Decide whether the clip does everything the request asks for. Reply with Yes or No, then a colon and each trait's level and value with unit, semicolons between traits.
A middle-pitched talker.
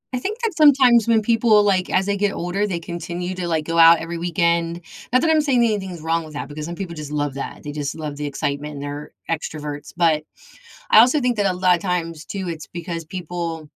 Yes: medium, 170 Hz